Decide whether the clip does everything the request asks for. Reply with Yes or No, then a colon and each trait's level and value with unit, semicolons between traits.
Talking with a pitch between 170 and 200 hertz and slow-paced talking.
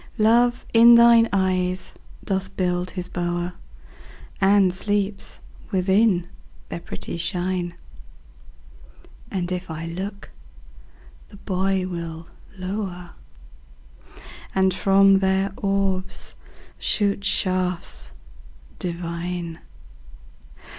Yes: medium, 185 Hz; slow, 85 wpm